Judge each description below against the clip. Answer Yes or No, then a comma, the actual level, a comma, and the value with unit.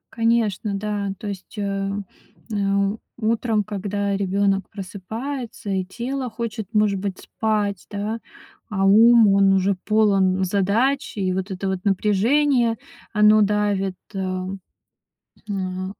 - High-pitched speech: Yes, high, 205 Hz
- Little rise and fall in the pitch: Yes, narrow, 2.2 semitones